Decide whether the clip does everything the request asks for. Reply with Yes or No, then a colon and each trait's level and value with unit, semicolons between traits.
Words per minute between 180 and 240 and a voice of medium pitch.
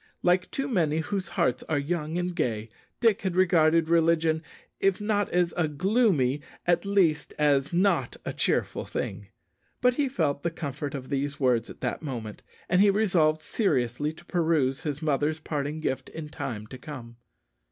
No: average, 170 wpm; medium, 160 Hz